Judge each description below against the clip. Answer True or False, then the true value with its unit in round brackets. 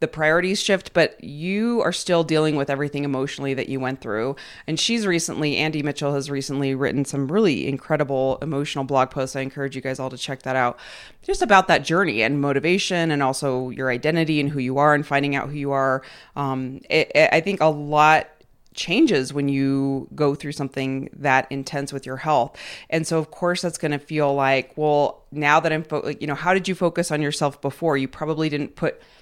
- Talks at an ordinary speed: False (215 wpm)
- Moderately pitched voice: True (145 Hz)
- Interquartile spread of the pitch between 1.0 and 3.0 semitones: True (2.6 semitones)